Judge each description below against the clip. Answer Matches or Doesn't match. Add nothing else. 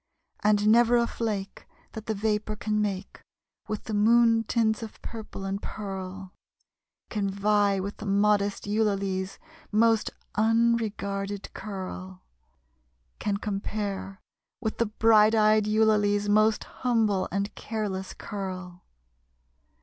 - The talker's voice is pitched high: Matches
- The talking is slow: Matches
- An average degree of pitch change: Doesn't match